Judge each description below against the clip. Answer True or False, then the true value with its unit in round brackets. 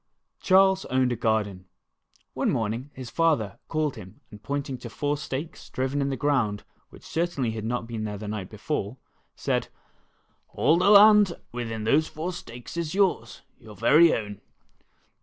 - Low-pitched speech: True (130 Hz)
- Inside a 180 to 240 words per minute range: False (160 wpm)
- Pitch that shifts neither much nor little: False (6.2 semitones)